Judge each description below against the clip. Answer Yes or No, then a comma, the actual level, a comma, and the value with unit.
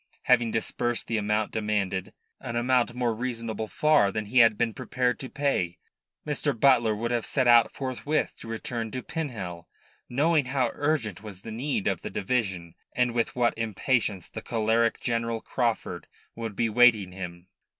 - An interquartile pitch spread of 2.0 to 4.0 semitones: Yes, average, 2.8 semitones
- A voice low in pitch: Yes, low, 115 Hz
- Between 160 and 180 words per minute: Yes, average, 165 wpm